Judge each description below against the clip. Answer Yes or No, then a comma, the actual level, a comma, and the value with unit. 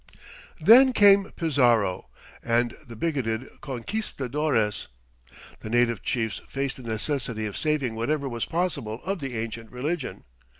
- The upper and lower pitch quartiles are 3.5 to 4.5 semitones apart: No, average, 5.1 semitones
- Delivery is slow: Yes, slow, 125 wpm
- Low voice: Yes, low, 125 Hz